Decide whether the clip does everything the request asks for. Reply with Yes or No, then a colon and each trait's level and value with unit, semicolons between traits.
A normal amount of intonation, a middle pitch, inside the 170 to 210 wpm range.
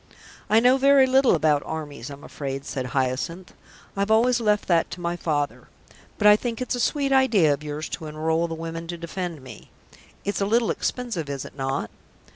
No: wide, 7.3 semitones; medium, 170 Hz; average, 195 wpm